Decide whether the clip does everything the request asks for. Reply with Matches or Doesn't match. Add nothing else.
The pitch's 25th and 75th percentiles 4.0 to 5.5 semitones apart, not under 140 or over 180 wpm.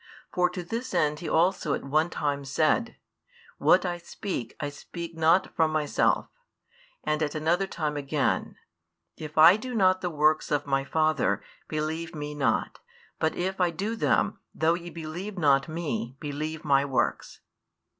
Doesn't match